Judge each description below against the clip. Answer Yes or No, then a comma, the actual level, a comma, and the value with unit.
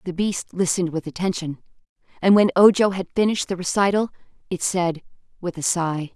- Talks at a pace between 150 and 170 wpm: Yes, average, 165 wpm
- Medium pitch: Yes, medium, 180 Hz